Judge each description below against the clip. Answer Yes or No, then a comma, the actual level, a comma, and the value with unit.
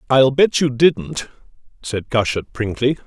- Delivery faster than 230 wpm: No, slow, 135 wpm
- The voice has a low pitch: Yes, low, 130 Hz